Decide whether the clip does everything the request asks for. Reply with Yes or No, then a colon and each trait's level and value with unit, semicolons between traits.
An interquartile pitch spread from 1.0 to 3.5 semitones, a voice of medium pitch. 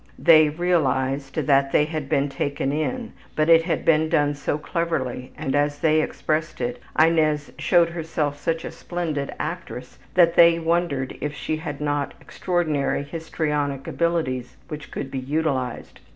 Yes: average, 2.8 semitones; medium, 150 Hz